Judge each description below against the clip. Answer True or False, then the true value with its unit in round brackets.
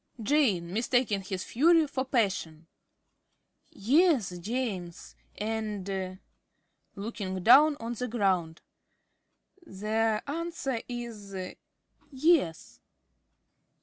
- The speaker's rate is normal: False (80 wpm)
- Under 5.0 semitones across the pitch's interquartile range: False (5.4 semitones)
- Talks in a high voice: True (220 Hz)